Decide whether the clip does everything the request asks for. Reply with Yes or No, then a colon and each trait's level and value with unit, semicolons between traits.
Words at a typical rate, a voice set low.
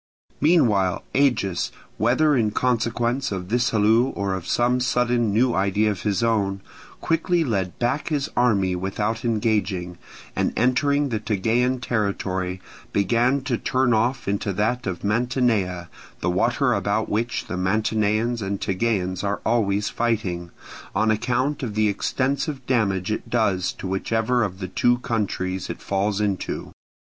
Yes: average, 145 wpm; low, 110 Hz